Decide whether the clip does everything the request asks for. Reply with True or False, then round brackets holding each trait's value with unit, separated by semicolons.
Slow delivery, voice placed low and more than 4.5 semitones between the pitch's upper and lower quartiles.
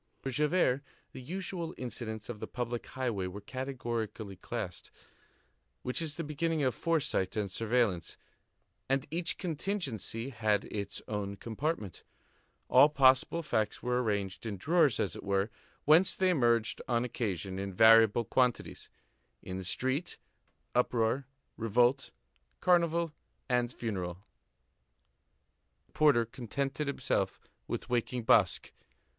True (125 wpm; 120 Hz; 5.1 semitones)